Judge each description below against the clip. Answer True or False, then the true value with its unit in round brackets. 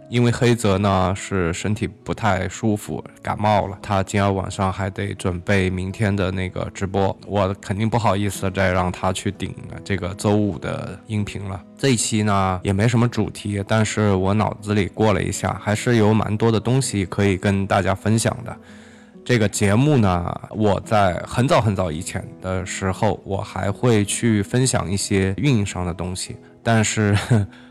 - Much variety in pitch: False (2.6 semitones)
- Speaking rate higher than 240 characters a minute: True (260 characters per minute)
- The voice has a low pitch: True (100 Hz)